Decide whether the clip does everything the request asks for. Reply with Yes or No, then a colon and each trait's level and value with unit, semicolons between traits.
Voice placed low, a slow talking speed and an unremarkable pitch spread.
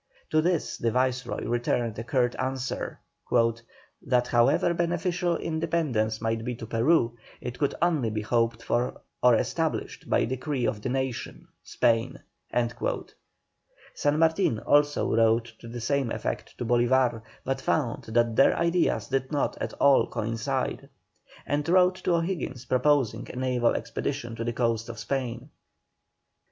No: low, 125 Hz; average, 145 wpm; average, 3.9 semitones